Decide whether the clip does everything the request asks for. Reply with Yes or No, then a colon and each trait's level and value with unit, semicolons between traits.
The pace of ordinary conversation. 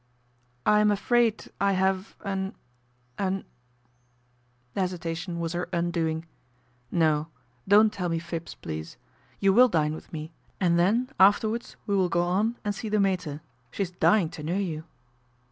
Yes: average, 165 wpm